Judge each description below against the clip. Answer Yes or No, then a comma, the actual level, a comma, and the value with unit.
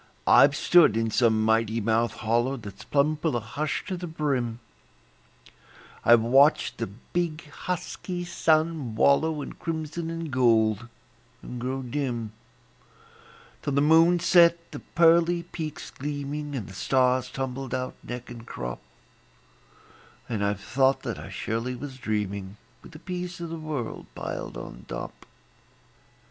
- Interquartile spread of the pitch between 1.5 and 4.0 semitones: No, wide, 5.5 semitones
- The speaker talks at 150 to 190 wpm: No, average, 140 wpm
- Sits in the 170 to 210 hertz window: No, low, 135 Hz